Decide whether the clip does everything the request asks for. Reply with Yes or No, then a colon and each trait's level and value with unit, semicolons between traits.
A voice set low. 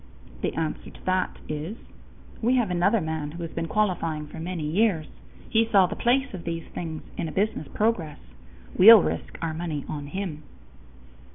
No: medium, 175 Hz